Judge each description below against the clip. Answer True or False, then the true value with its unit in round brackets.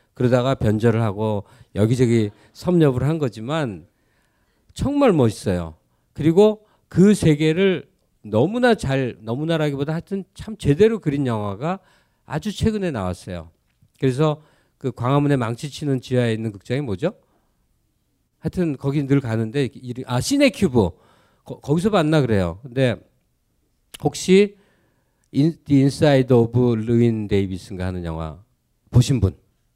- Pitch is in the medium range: False (130 Hz)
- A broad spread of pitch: True (6.3 semitones)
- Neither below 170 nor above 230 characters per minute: False (270 characters per minute)